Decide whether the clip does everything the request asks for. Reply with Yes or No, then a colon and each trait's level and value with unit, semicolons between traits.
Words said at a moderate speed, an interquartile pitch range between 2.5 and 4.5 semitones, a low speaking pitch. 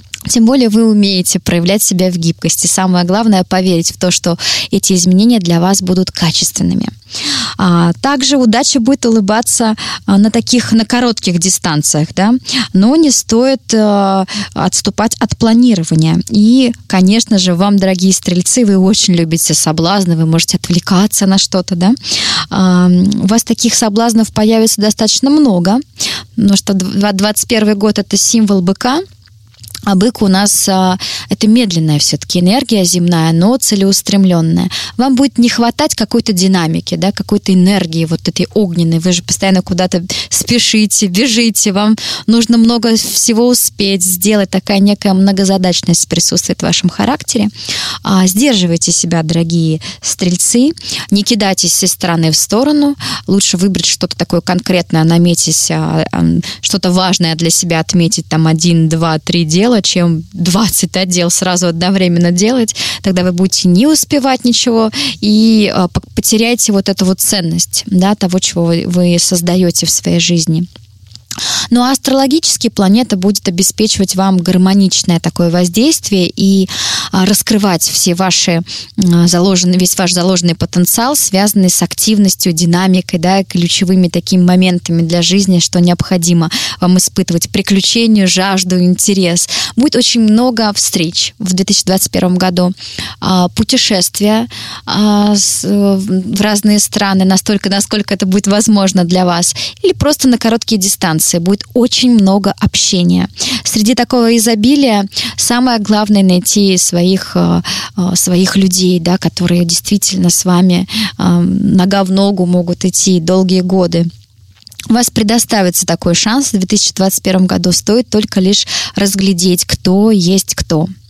No: average, 130 wpm; average, 3.3 semitones; high, 190 Hz